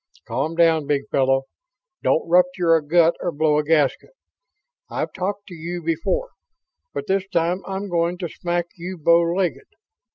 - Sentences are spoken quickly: No, average, 160 wpm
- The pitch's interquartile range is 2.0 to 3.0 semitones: Yes, narrow, 2.4 semitones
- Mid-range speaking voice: Yes, medium, 170 Hz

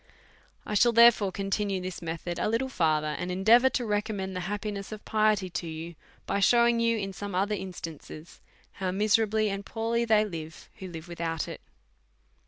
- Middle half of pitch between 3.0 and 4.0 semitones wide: Yes, average, 3.6 semitones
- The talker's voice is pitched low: No, high, 200 Hz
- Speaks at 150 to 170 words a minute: No, average, 190 wpm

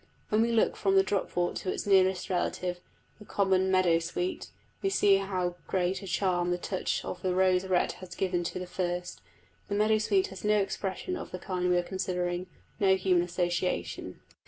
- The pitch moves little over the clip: Yes, narrow, 1.5 semitones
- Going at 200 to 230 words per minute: No, average, 185 wpm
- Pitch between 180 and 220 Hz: Yes, medium, 185 Hz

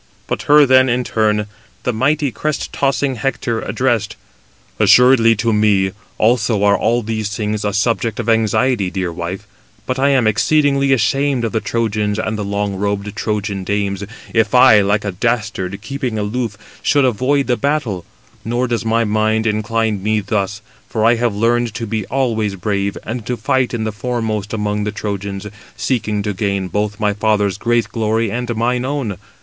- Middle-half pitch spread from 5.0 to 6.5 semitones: No, average, 2.8 semitones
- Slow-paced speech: No, average, 175 wpm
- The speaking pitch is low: Yes, low, 110 Hz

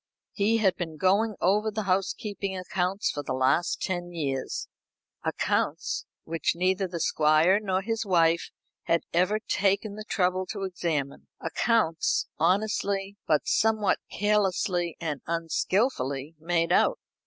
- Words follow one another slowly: Yes, slow, 130 wpm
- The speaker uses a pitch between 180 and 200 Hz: Yes, medium, 185 Hz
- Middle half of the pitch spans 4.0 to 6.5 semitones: No, average, 3.5 semitones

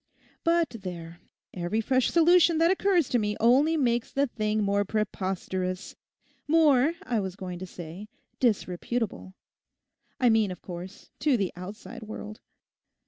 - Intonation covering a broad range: Yes, wide, 6.2 semitones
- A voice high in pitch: Yes, high, 215 Hz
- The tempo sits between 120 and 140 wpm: Yes, slow, 135 wpm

